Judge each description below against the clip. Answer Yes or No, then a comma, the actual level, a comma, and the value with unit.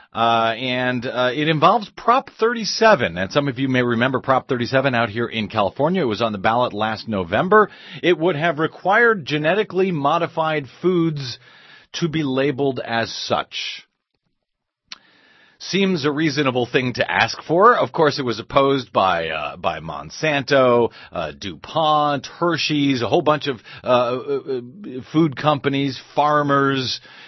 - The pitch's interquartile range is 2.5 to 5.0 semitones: Yes, average, 4.5 semitones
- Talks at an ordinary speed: Yes, average, 145 wpm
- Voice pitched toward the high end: No, medium, 140 Hz